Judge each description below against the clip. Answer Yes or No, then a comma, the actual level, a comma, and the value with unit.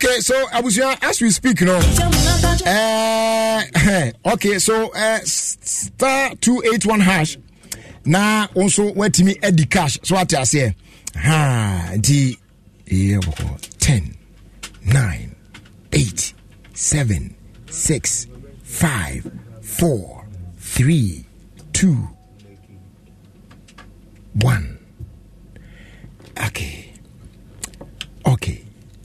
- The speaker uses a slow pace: Yes, slow, 90 wpm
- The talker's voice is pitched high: No, low, 135 Hz